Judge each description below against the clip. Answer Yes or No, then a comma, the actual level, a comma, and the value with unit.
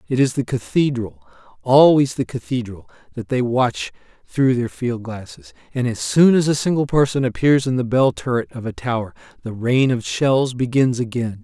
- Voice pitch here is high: No, low, 125 Hz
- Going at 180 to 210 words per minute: Yes, average, 185 wpm